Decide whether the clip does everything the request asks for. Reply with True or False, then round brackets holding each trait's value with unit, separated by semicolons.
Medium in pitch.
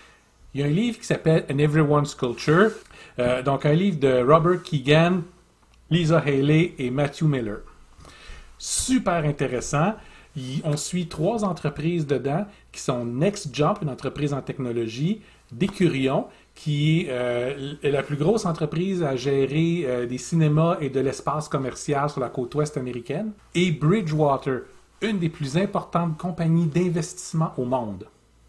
True (150 Hz)